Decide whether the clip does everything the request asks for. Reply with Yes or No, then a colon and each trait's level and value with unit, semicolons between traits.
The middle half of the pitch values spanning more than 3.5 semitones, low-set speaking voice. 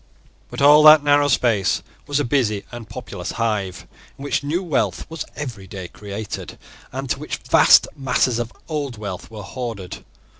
Yes: wide, 5.5 semitones; low, 120 Hz